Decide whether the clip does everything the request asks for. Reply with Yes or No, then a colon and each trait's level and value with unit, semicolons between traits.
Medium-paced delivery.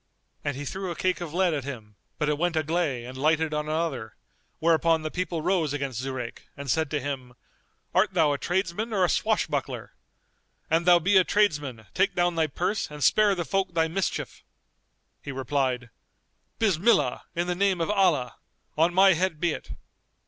Yes: average, 185 wpm